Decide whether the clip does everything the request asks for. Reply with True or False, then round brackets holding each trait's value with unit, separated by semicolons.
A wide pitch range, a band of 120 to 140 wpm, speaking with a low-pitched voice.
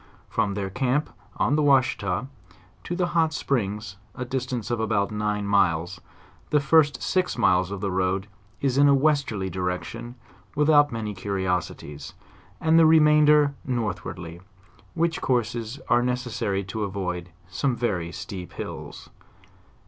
True (6.7 semitones; 135 wpm; 115 Hz)